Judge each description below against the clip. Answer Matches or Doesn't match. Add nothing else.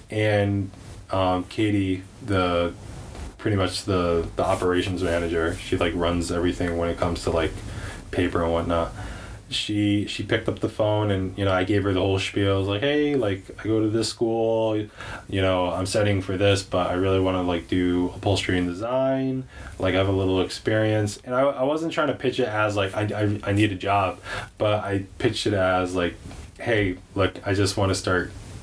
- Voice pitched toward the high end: Doesn't match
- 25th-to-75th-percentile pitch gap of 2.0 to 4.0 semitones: Matches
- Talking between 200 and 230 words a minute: Matches